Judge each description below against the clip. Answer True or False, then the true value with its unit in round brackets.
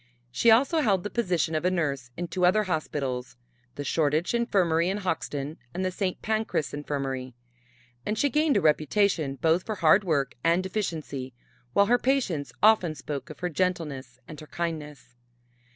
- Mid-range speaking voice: True (170 Hz)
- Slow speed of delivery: False (170 wpm)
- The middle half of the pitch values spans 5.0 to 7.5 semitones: True (5.4 semitones)